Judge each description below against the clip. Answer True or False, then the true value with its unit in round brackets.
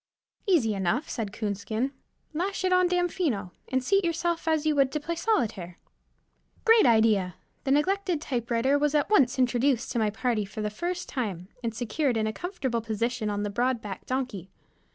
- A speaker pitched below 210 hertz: False (250 Hz)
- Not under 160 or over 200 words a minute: True (175 wpm)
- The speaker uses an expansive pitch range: True (6.6 semitones)